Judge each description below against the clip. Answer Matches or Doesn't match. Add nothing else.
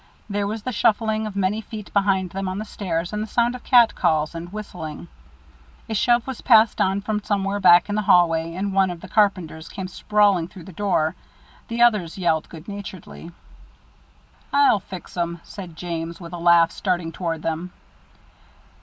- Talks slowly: Doesn't match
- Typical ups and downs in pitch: Matches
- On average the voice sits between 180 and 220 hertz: Matches